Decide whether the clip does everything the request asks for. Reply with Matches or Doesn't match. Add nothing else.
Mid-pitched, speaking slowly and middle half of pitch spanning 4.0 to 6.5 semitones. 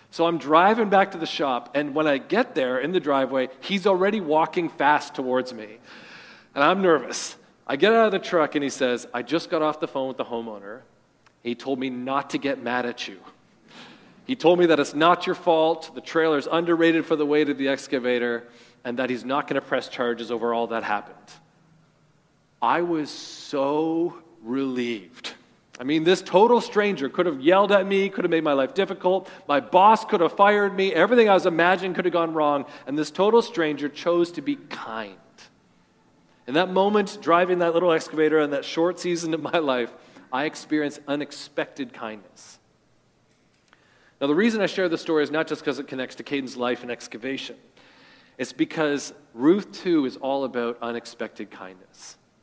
Doesn't match